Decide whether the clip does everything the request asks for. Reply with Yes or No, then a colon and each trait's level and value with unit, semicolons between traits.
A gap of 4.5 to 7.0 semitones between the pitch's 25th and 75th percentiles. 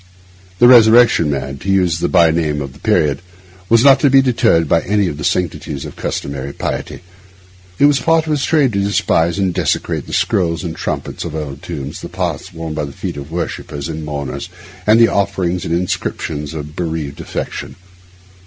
Yes: wide, 5.4 semitones